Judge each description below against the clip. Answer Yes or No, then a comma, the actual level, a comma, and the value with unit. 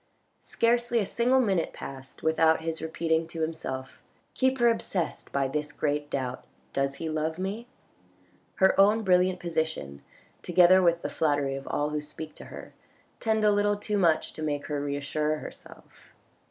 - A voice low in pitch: No, medium, 160 Hz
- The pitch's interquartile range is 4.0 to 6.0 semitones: Yes, average, 4.8 semitones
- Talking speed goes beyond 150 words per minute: Yes, average, 170 wpm